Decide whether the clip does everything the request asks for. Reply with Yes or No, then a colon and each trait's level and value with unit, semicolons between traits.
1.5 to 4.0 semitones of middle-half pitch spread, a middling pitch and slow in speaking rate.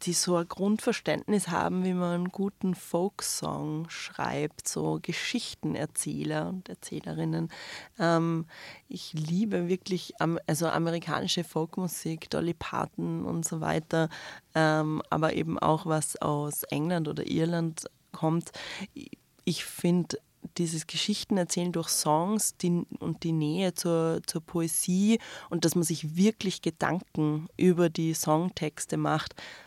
Yes: average, 2.7 semitones; medium, 165 Hz; slow, 115 wpm